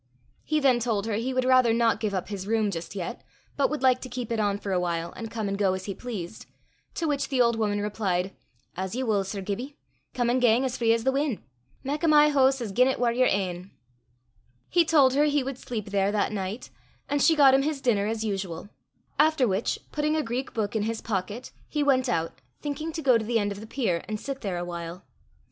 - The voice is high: Yes, high, 230 Hz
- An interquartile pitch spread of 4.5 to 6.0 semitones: Yes, average, 4.8 semitones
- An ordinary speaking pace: No, fast, 240 wpm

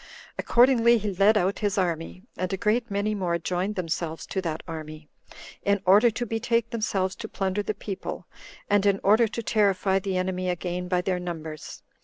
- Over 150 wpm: Yes, average, 180 wpm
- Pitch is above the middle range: Yes, high, 195 Hz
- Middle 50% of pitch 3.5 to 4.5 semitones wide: No, average, 2.9 semitones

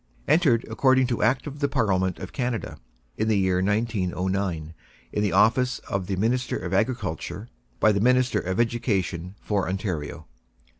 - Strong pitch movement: No, average, 4.8 semitones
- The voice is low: Yes, low, 105 Hz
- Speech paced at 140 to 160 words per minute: Yes, average, 155 wpm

